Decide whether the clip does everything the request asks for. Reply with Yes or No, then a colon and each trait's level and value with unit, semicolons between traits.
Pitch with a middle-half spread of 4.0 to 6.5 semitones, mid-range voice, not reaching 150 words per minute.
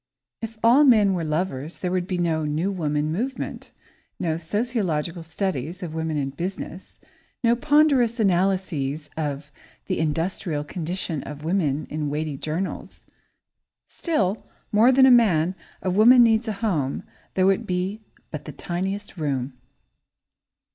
Yes: average, 5.1 semitones; medium, 180 Hz; average, 140 wpm